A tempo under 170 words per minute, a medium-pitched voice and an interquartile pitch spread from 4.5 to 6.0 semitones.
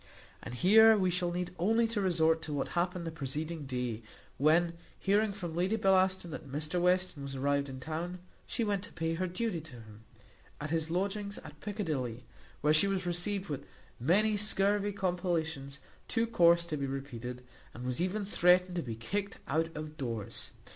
No: average, 180 wpm; medium, 170 Hz; average, 4.9 semitones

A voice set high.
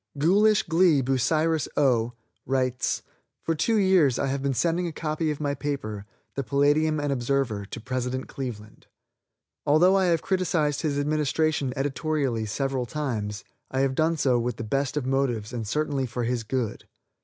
No: medium, 140 Hz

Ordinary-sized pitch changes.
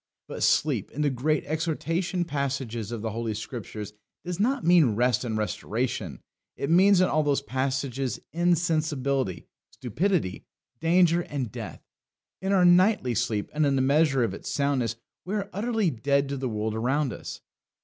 No: wide, 6.1 semitones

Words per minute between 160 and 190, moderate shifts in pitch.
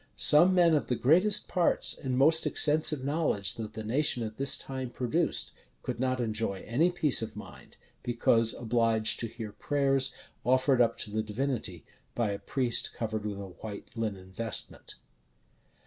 Yes: average, 165 wpm; average, 4.4 semitones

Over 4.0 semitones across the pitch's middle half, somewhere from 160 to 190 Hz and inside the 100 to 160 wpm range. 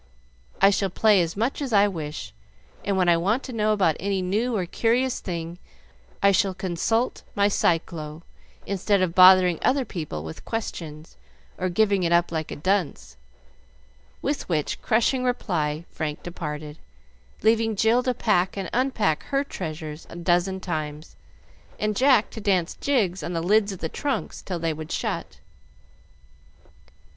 Yes: average, 4.6 semitones; medium, 185 Hz; average, 155 wpm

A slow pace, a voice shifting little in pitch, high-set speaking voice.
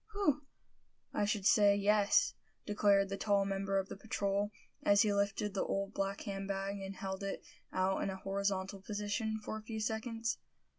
No: average, 180 wpm; narrow, 1.1 semitones; high, 200 Hz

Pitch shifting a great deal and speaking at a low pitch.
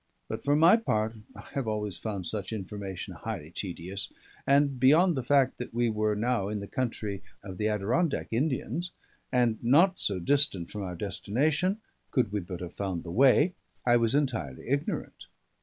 Yes: wide, 5.8 semitones; low, 115 Hz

